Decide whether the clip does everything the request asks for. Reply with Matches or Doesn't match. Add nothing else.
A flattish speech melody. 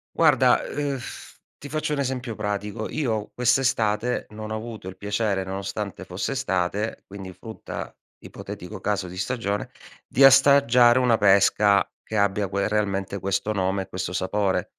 Doesn't match